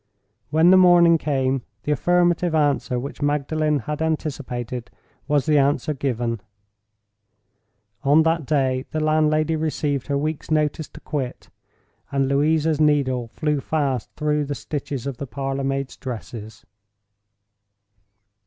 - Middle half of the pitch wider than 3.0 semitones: No, narrow, 2.4 semitones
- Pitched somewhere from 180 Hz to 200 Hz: No, medium, 145 Hz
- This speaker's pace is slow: Yes, slow, 125 wpm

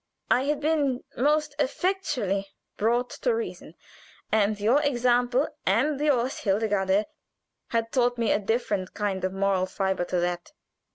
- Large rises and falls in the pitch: Yes, wide, 6.0 semitones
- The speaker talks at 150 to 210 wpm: No, slow, 135 wpm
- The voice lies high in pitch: Yes, high, 235 Hz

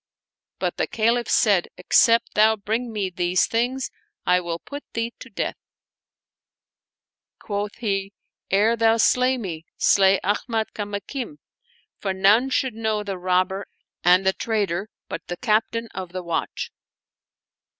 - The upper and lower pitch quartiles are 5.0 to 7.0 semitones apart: No, average, 3.3 semitones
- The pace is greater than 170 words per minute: No, average, 145 wpm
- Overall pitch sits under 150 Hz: No, high, 210 Hz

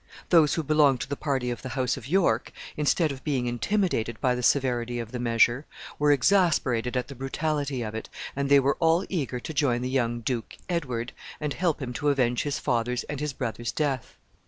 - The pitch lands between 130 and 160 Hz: Yes, low, 135 Hz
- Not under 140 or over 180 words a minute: No, fast, 205 wpm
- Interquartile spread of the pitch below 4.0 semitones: Yes, average, 3.5 semitones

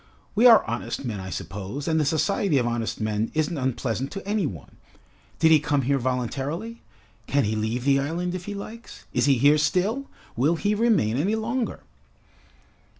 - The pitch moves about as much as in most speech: No, wide, 8.2 semitones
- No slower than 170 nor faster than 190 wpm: Yes, average, 180 wpm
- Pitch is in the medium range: Yes, medium, 145 Hz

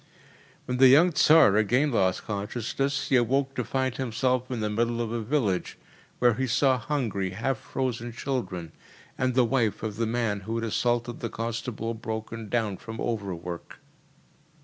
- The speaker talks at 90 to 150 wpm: No, average, 165 wpm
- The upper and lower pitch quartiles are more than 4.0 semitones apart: No, average, 2.9 semitones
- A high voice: No, low, 115 Hz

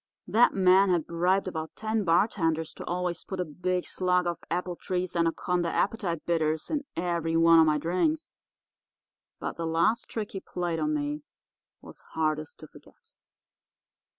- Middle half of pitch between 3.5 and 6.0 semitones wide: No, average, 2.7 semitones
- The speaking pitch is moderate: Yes, medium, 180 Hz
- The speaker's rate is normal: Yes, average, 150 wpm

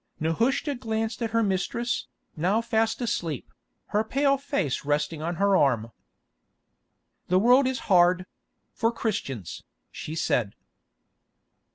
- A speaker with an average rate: No, slow, 110 wpm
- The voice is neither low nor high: No, high, 205 Hz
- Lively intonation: Yes, wide, 6.4 semitones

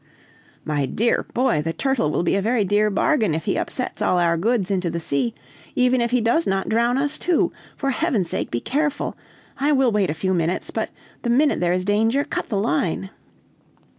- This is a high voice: Yes, high, 215 Hz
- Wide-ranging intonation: Yes, wide, 6.2 semitones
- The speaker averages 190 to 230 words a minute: Yes, fast, 205 wpm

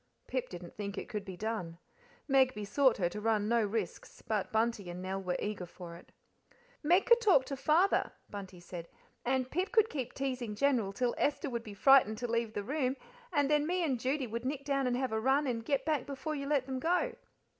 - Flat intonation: No, average, 5.0 semitones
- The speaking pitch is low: No, very high, 250 Hz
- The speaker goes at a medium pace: No, fast, 220 wpm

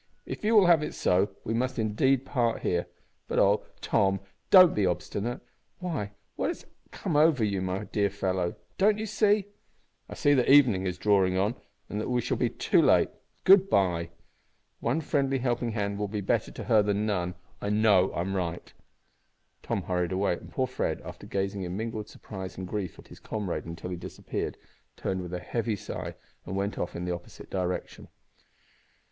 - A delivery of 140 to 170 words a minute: No, average, 190 wpm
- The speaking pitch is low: Yes, low, 105 Hz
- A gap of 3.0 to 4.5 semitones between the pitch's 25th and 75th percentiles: No, average, 5.3 semitones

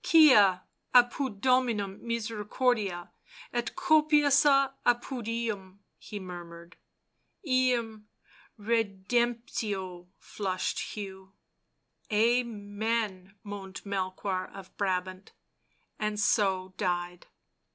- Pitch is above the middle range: Yes, high, 210 Hz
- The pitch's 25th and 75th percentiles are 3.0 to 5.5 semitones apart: Yes, average, 4.1 semitones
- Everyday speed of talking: No, slow, 85 wpm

